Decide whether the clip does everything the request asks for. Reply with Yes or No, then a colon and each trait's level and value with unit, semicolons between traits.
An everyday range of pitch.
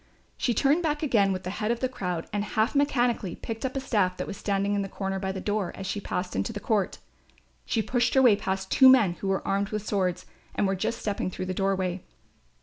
Yes: average, 3.7 semitones